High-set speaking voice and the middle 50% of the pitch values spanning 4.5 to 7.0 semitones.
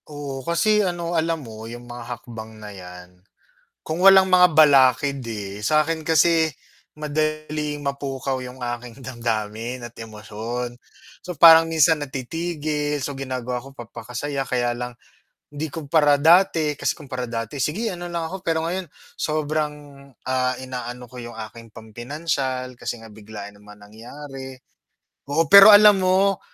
No: low, 135 Hz; average, 5.0 semitones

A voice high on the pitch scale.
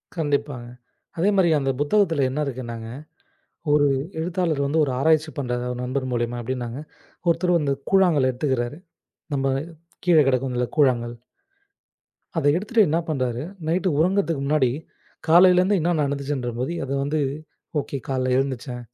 No: medium, 140 Hz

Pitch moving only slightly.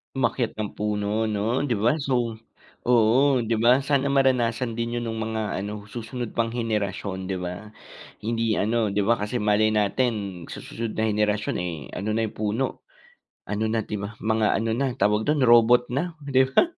Yes: narrow, 2.3 semitones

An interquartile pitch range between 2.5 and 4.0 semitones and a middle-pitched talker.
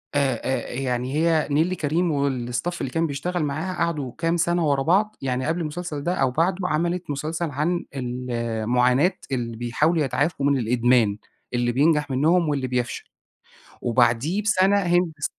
No: average, 5.3 semitones; medium, 145 Hz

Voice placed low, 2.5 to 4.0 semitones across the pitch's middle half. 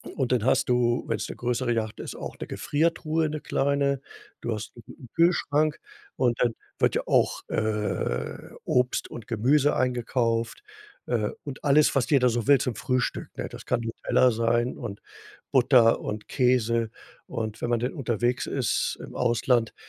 Yes: low, 120 Hz; average, 2.9 semitones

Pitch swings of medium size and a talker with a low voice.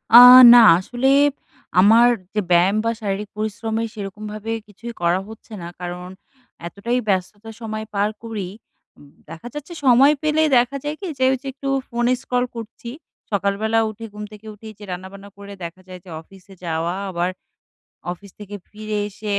No: average, 3.2 semitones; high, 210 Hz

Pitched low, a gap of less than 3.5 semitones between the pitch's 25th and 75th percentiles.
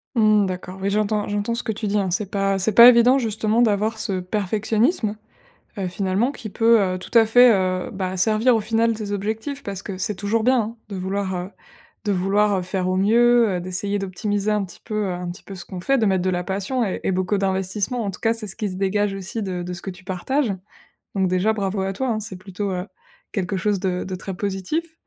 No: high, 200 Hz; average, 2.8 semitones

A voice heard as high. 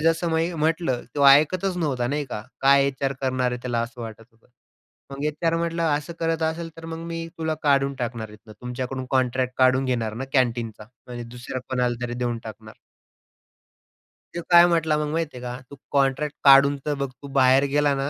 No: low, 135 Hz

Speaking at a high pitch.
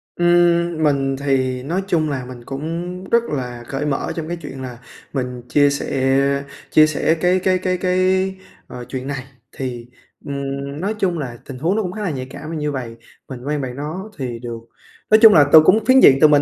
No: medium, 145 Hz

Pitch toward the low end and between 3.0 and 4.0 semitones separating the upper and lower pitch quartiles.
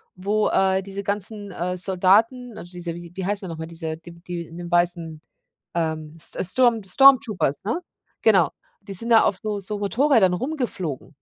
No: high, 190 Hz; average, 3.7 semitones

